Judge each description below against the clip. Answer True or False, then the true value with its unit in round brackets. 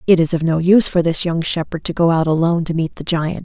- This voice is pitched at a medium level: True (165 Hz)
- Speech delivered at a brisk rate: True (295 wpm)